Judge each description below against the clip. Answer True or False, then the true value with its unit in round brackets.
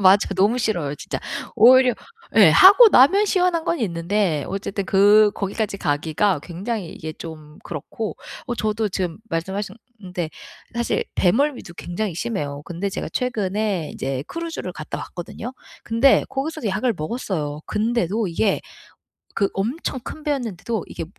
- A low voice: False (205 Hz)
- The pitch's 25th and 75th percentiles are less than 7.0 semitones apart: True (5.4 semitones)